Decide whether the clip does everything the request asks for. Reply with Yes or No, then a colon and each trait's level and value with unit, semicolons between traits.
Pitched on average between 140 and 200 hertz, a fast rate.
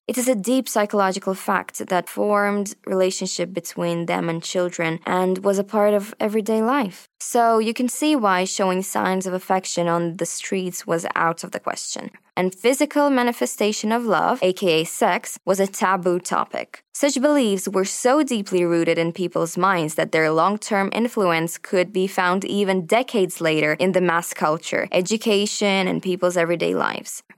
No: high, 190 Hz; average, 165 wpm